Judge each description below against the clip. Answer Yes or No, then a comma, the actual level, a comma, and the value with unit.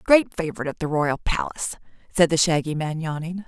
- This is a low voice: No, medium, 165 Hz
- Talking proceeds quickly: No, average, 190 wpm